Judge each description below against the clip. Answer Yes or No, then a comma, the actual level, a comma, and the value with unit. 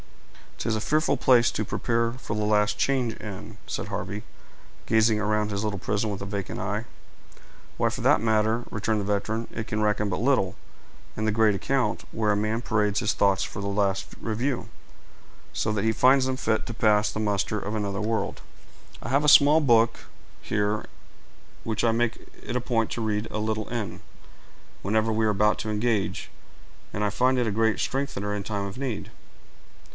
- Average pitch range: No, narrow, 1.9 semitones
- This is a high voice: No, low, 110 Hz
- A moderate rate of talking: Yes, average, 195 wpm